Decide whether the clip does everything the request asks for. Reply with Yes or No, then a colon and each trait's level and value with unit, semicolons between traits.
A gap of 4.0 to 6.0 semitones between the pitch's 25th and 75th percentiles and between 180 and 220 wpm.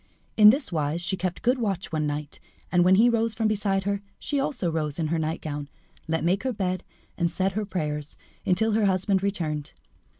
Yes: average, 4.7 semitones; average, 200 wpm